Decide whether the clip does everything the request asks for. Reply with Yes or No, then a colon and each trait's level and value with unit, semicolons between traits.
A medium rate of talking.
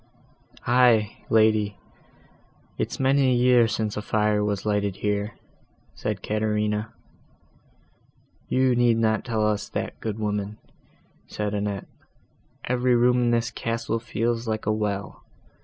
No: slow, 125 wpm